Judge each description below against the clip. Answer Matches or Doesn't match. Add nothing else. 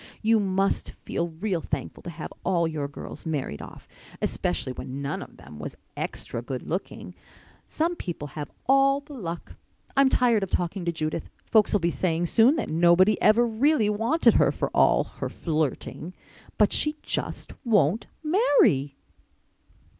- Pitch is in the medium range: Matches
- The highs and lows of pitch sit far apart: Matches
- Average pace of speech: Matches